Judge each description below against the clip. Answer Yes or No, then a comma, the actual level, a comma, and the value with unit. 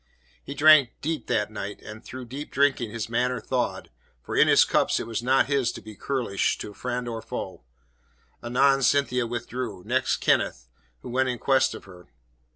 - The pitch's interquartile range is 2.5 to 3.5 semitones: Yes, average, 3.0 semitones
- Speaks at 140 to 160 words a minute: No, average, 180 wpm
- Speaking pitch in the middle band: No, low, 125 Hz